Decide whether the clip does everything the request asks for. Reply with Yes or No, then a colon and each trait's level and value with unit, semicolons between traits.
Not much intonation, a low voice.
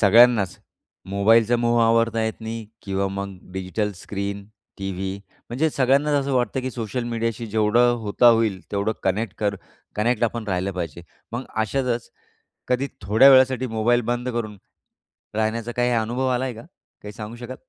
No: average, 3.1 semitones; low, 115 Hz